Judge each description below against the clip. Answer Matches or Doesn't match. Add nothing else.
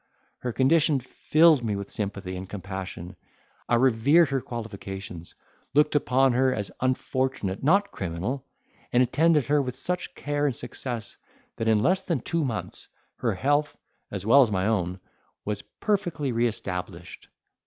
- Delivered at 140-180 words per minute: Matches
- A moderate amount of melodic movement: Doesn't match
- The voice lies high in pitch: Doesn't match